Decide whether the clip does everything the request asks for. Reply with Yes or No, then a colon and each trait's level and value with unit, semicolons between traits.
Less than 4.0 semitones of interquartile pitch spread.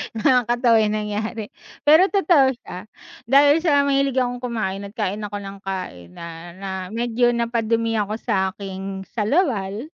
No: average, 4.4 semitones